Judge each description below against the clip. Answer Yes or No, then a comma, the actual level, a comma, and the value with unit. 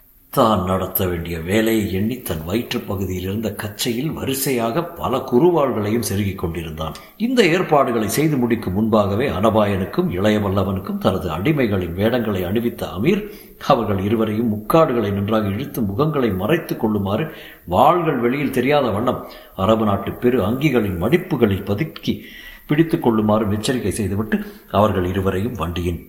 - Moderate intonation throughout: Yes, average, 4.3 semitones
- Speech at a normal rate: Yes, average, 120 wpm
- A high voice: No, low, 110 Hz